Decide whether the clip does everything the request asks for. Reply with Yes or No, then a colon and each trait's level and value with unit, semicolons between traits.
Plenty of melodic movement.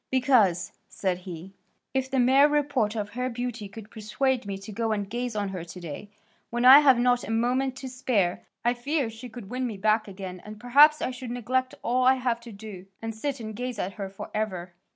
No: average, 3.9 semitones